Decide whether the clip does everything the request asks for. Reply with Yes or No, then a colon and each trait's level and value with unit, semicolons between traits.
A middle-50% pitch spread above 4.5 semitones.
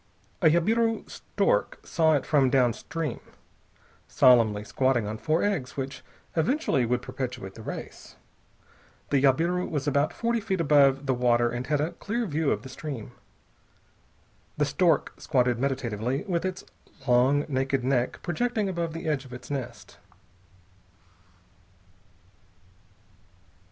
Yes: average, 4.9 semitones